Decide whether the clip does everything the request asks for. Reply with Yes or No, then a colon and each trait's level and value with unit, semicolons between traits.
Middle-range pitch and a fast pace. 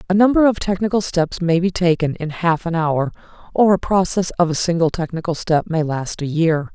Yes: medium, 170 Hz; fast, 215 wpm